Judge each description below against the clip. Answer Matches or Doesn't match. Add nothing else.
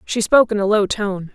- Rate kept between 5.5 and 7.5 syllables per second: Matches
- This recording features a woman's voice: Matches